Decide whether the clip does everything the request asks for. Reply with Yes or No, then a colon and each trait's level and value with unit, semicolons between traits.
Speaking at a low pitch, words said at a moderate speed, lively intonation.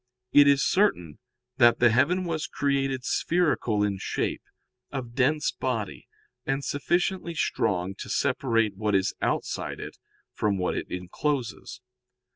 No: low, 130 Hz; slow, 130 wpm; wide, 5.7 semitones